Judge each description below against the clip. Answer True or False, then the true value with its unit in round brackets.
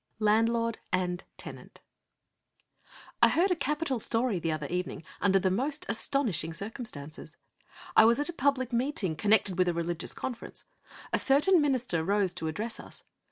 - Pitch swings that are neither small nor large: False (6.5 semitones)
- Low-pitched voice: False (220 Hz)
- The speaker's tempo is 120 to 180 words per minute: True (160 wpm)